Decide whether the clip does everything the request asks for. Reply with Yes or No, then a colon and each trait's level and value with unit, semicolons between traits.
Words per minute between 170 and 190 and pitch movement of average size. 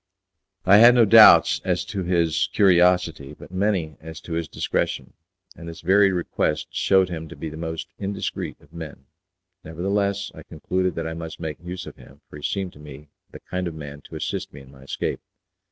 No: average, 200 wpm; average, 3.2 semitones